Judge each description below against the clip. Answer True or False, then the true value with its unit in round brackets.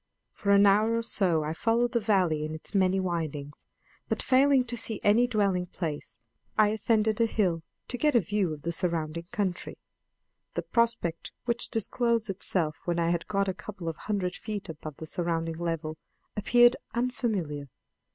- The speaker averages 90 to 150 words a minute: False (170 wpm)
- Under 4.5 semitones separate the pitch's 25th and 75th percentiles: False (5.3 semitones)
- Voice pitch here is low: False (195 Hz)